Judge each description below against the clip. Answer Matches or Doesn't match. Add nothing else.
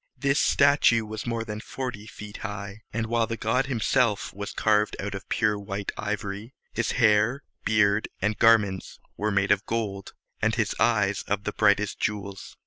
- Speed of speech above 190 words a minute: Doesn't match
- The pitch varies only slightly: Matches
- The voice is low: Matches